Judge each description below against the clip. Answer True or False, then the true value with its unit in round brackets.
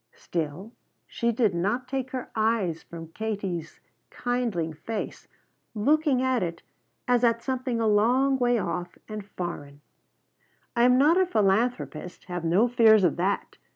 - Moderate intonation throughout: False (5.8 semitones)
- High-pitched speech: True (220 Hz)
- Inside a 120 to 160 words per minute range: True (145 wpm)